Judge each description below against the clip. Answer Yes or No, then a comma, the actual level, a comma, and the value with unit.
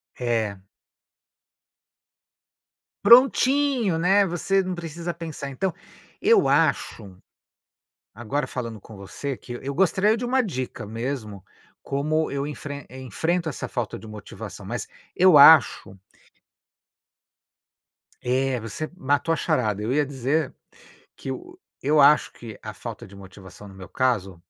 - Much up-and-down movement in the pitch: Yes, wide, 6.7 semitones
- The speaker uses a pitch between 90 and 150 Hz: Yes, medium, 140 Hz